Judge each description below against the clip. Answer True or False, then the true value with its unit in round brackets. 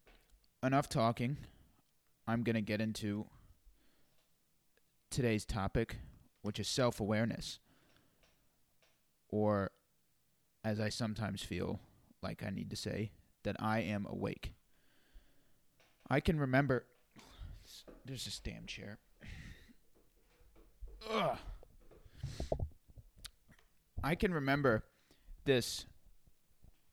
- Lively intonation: False (3.3 semitones)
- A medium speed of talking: False (85 wpm)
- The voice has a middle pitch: False (110 Hz)